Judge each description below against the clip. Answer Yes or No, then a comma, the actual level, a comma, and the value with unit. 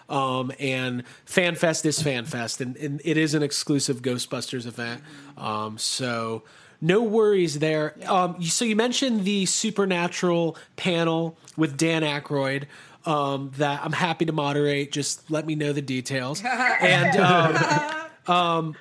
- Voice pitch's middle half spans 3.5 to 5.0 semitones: Yes, average, 4.0 semitones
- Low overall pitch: No, medium, 155 Hz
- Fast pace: No, slow, 135 wpm